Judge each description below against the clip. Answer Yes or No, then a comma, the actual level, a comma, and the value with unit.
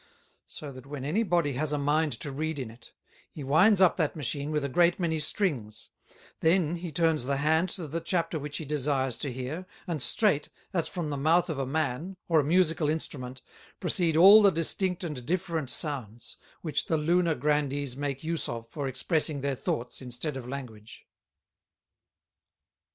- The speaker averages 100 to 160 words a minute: No, average, 180 wpm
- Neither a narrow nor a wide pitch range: Yes, average, 3.5 semitones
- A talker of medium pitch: Yes, medium, 150 Hz